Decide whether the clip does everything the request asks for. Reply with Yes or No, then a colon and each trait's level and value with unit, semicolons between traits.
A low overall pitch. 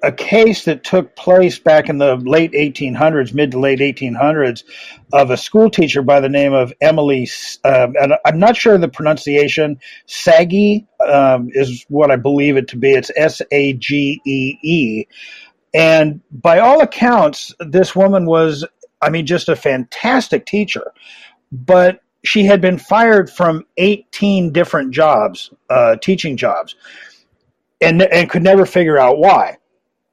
No: medium, 160 Hz